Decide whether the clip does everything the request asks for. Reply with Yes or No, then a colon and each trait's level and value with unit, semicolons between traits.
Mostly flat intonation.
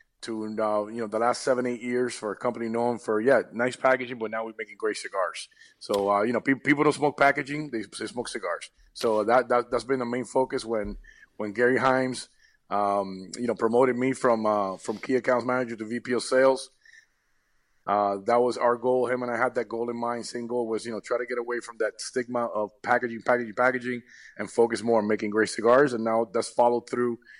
Yes: narrow, 2.3 semitones